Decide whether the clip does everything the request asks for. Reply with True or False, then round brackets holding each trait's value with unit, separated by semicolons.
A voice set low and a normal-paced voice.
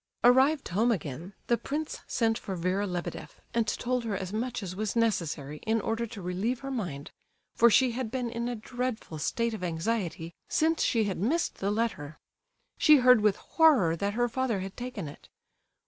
False (225 Hz; 185 wpm)